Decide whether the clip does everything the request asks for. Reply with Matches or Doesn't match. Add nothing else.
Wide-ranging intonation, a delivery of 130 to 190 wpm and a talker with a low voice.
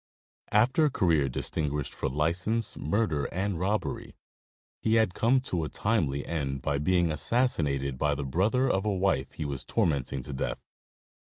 Matches